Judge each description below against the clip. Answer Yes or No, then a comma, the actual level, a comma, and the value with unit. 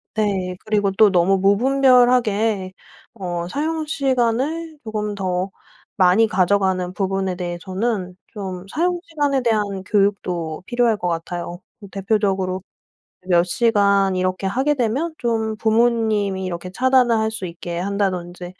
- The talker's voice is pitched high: Yes, high, 200 Hz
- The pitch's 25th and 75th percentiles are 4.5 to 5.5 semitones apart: No, average, 4.1 semitones